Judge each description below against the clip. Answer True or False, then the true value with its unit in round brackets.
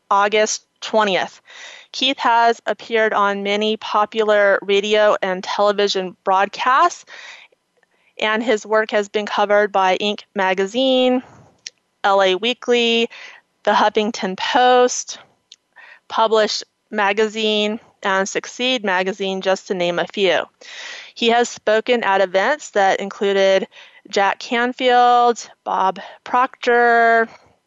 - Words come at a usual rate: False (100 wpm)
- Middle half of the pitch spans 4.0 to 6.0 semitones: False (3.6 semitones)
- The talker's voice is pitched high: True (215 Hz)